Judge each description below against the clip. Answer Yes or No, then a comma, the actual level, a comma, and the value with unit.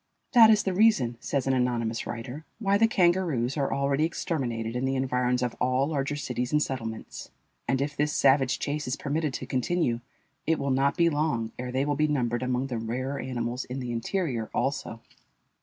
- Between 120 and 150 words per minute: No, average, 190 wpm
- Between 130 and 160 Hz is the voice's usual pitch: Yes, low, 135 Hz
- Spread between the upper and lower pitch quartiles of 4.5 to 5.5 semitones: No, average, 3.4 semitones